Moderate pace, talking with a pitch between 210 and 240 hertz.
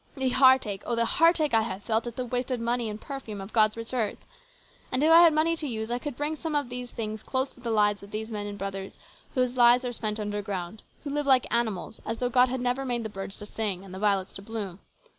No: fast, 260 wpm; high, 235 Hz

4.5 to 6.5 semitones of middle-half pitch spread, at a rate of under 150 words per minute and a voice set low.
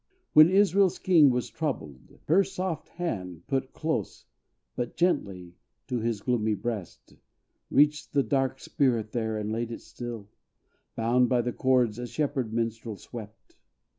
Yes: average, 5.1 semitones; average, 140 wpm; low, 120 Hz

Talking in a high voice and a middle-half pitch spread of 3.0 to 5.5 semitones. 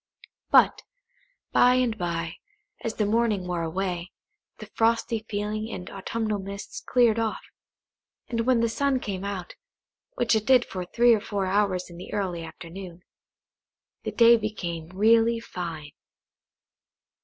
Yes: high, 205 Hz; average, 4.2 semitones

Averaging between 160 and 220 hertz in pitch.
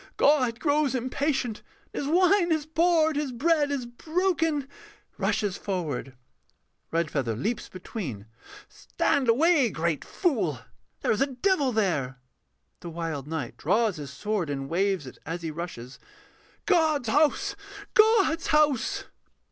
No: high, 240 Hz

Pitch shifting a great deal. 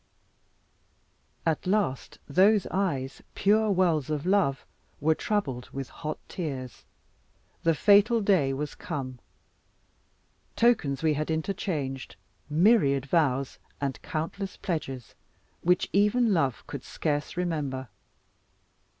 Yes: wide, 6.1 semitones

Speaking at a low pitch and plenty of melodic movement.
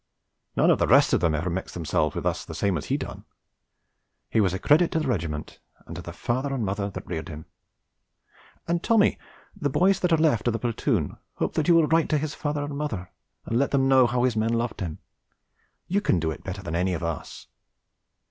Yes: low, 115 Hz; wide, 8.8 semitones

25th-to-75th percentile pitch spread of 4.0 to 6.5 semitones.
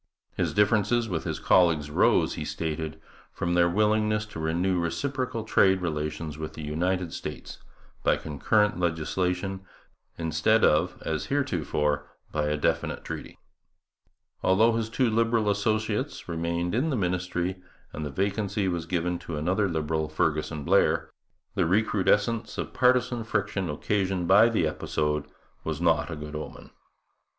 Yes: average, 5.0 semitones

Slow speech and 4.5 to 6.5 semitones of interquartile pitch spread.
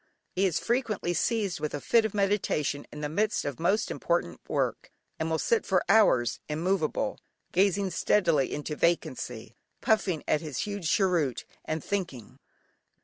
No: average, 150 wpm; average, 5.1 semitones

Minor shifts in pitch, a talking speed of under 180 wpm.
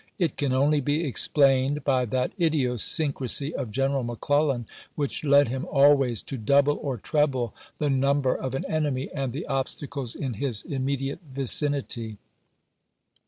Yes: narrow, 2.0 semitones; average, 145 wpm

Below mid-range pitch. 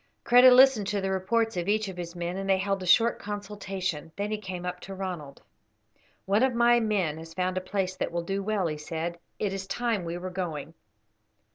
No: high, 190 Hz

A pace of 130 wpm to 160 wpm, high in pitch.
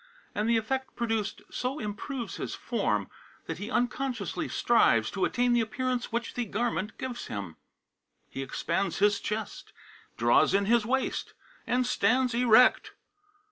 Yes: average, 140 wpm; high, 235 Hz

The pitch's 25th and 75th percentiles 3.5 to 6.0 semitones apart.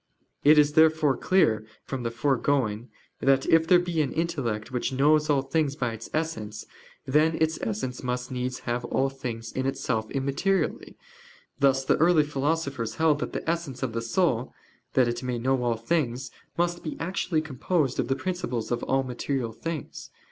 Yes: average, 4.3 semitones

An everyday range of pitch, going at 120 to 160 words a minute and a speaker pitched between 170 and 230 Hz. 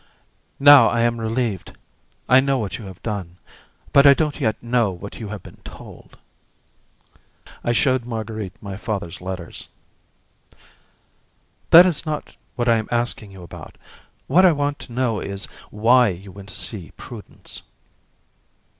No: average, 4.5 semitones; average, 150 wpm; low, 115 Hz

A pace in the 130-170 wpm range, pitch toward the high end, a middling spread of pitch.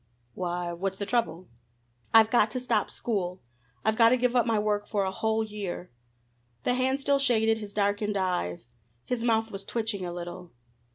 No: average, 180 wpm; high, 210 Hz; average, 3.5 semitones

